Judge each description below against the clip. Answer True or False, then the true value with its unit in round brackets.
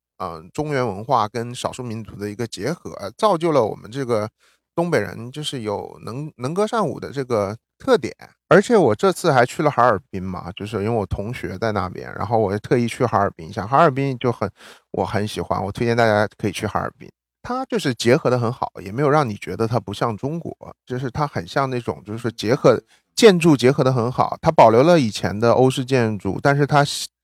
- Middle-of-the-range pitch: False (120 Hz)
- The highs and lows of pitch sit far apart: False (4.9 semitones)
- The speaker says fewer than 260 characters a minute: False (315 characters per minute)